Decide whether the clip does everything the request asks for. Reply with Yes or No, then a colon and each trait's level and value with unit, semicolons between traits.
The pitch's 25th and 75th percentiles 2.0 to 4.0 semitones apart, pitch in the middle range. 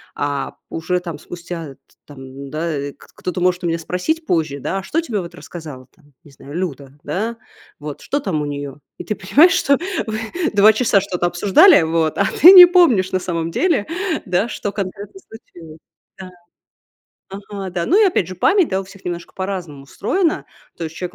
No: average, 4.5 semitones; medium, 180 Hz